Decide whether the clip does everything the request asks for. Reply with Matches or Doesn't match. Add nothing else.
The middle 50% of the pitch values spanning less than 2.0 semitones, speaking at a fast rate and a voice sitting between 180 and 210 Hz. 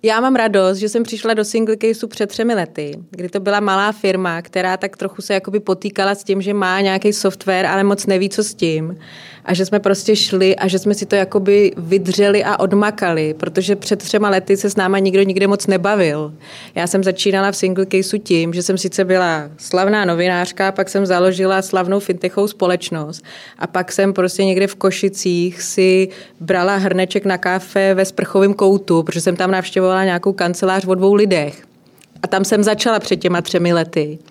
Matches